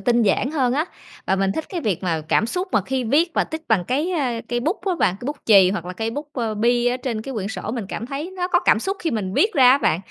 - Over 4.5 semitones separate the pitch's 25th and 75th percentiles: Yes, wide, 5.5 semitones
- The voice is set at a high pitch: Yes, high, 245 Hz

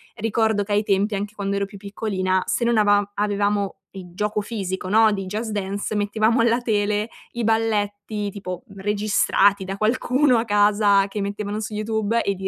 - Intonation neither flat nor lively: No, narrow, 1.6 semitones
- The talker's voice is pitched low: No, high, 205 Hz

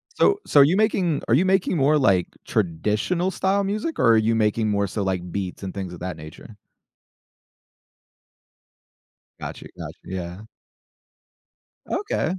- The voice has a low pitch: Yes, low, 110 Hz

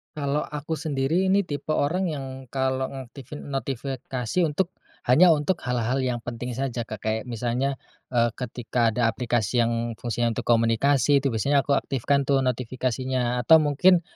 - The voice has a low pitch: Yes, low, 130 Hz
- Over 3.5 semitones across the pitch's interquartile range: No, average, 3.2 semitones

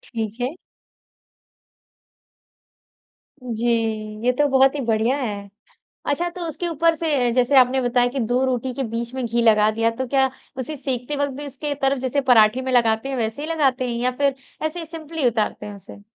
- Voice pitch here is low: No, very high, 255 Hz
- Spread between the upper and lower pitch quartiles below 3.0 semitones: No, average, 3.3 semitones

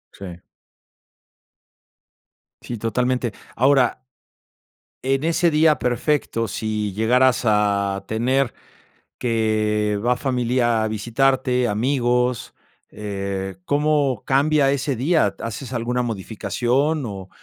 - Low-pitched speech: Yes, low, 120 Hz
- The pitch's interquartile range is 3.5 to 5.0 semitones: Yes, average, 3.9 semitones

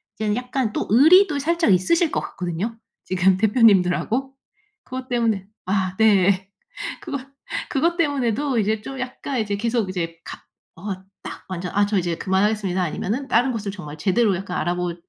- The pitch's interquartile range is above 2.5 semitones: Yes, wide, 5.5 semitones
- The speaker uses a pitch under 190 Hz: No, high, 210 Hz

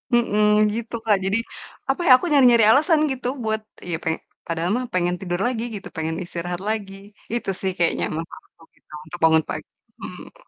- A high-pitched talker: Yes, high, 210 Hz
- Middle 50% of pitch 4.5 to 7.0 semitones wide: Yes, average, 5.3 semitones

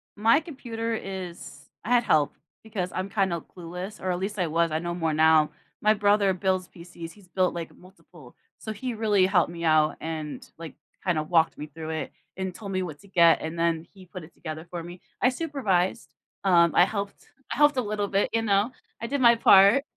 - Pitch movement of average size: Yes, average, 3.8 semitones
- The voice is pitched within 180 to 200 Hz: Yes, medium, 185 Hz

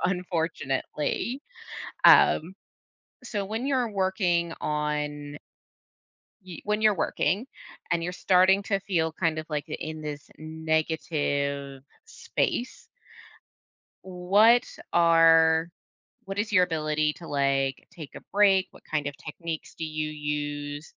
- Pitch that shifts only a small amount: No, average, 4.0 semitones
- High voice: No, medium, 165 Hz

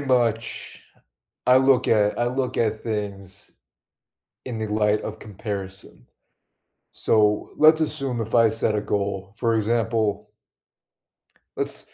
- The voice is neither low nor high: No, low, 110 Hz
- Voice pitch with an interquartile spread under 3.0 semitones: Yes, narrow, 2.4 semitones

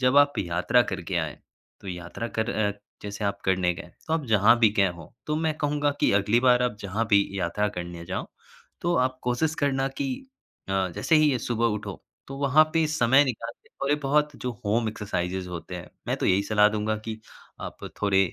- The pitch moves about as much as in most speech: No, wide, 5.9 semitones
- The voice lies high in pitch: No, low, 110 Hz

